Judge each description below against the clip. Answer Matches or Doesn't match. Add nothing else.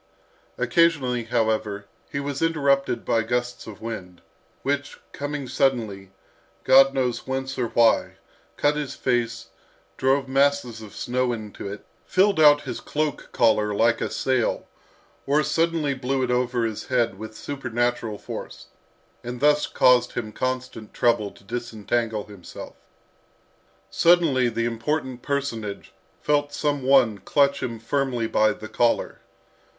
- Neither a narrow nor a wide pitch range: Matches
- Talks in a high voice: Doesn't match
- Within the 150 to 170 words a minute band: Doesn't match